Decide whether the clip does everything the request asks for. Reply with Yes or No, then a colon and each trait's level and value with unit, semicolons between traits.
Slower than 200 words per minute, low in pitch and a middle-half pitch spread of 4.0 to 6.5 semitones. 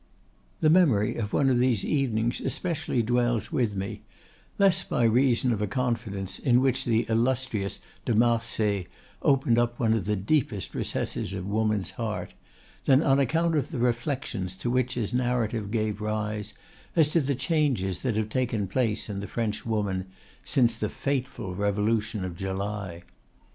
No: average, 160 wpm; low, 115 Hz; average, 3.6 semitones